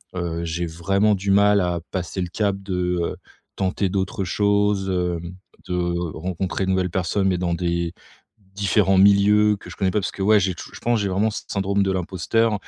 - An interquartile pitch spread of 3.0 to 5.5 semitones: No, narrow, 2.4 semitones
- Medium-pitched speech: No, very low, 95 Hz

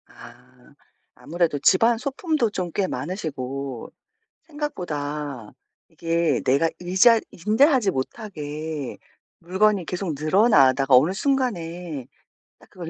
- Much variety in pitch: Yes, wide, 6.7 semitones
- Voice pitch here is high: No, medium, 170 Hz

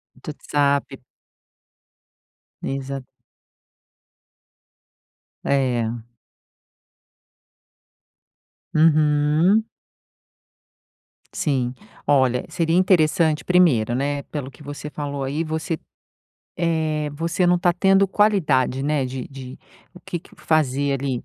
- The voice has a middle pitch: Yes, medium, 150 Hz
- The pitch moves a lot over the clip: No, average, 3.4 semitones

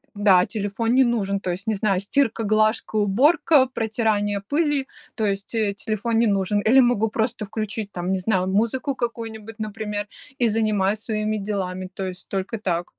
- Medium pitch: No, high, 215 Hz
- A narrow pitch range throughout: Yes, narrow, 2.3 semitones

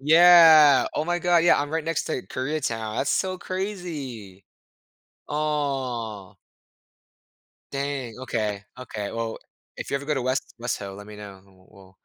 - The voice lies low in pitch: Yes, low, 130 Hz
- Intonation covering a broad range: Yes, wide, 6.3 semitones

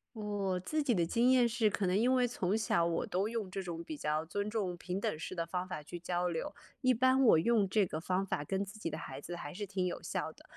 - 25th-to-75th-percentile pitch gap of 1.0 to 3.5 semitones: No, average, 4.2 semitones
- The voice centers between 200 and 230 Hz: No, high, 190 Hz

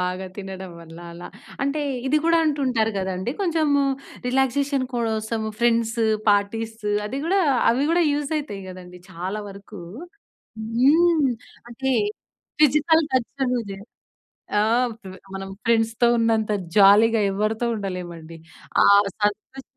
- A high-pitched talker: Yes, high, 225 Hz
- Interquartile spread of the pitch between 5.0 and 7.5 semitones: Yes, wide, 5.5 semitones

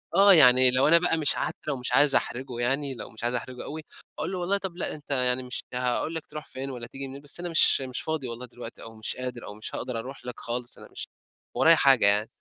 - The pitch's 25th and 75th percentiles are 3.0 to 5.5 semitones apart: Yes, average, 3.6 semitones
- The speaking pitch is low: Yes, low, 130 Hz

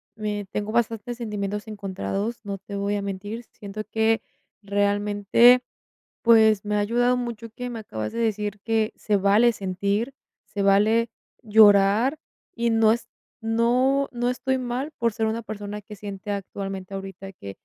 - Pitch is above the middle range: Yes, high, 215 Hz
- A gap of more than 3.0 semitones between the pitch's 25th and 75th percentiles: No, narrow, 2.5 semitones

